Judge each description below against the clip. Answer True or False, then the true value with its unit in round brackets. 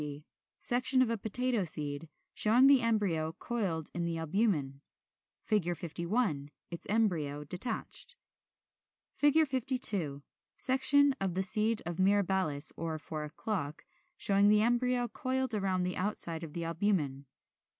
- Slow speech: True (130 wpm)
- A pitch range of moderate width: False (6.2 semitones)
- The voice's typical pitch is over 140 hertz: True (190 Hz)